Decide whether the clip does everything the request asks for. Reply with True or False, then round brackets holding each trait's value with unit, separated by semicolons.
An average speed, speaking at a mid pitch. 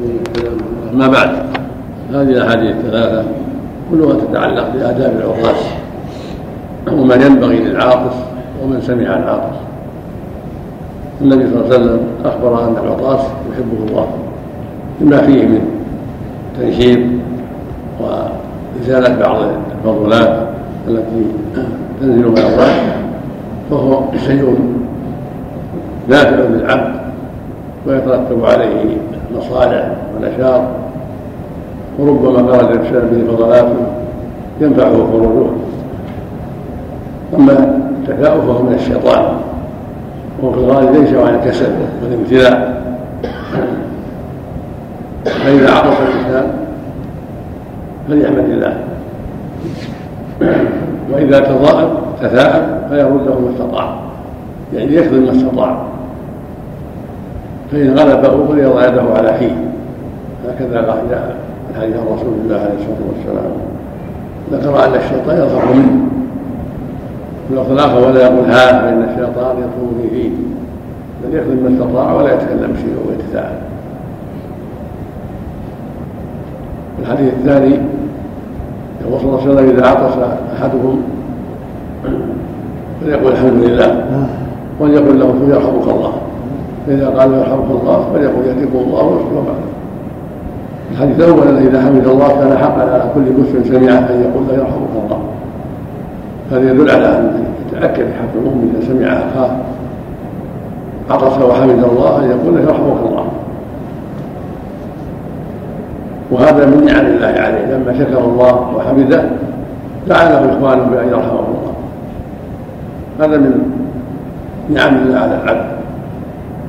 False (100 wpm; 130 Hz)